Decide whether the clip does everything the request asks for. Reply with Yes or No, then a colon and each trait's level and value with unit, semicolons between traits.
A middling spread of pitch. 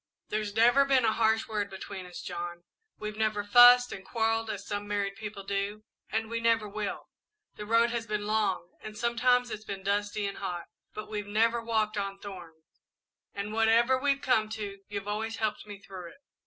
No: narrow, 2.0 semitones